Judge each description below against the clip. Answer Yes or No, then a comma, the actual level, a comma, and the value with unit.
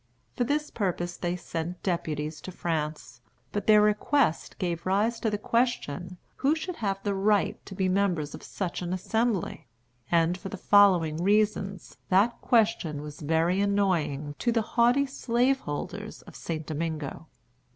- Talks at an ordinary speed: Yes, average, 150 wpm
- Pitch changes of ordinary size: Yes, average, 4.5 semitones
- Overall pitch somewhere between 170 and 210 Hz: Yes, high, 190 Hz